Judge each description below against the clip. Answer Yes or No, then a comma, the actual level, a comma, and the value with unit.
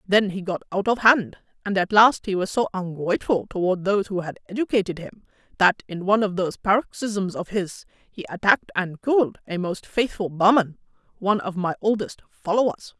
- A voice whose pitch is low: No, high, 195 Hz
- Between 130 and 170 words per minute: No, average, 185 wpm